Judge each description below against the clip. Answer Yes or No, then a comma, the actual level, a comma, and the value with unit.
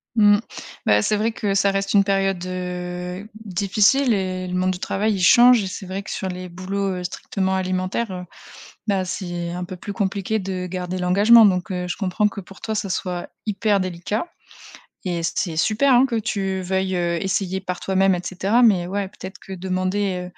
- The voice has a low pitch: No, high, 190 Hz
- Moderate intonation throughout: No, narrow, 1.9 semitones